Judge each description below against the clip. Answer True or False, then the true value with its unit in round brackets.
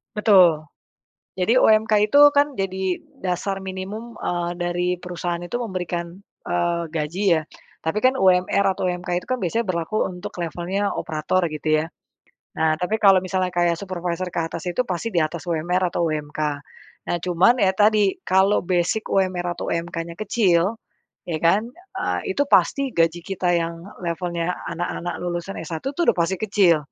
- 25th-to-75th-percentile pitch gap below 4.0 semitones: True (2.4 semitones)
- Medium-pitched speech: True (180 Hz)